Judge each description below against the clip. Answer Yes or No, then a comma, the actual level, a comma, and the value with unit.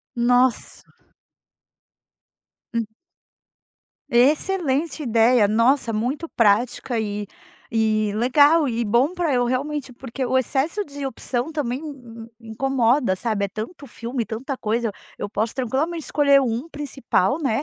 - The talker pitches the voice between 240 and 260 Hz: Yes, very high, 250 Hz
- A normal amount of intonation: Yes, average, 3.9 semitones